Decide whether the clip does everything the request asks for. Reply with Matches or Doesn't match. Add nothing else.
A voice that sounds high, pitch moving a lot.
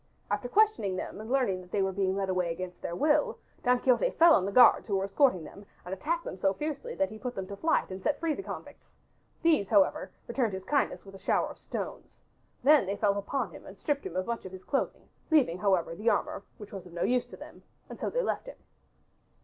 Matches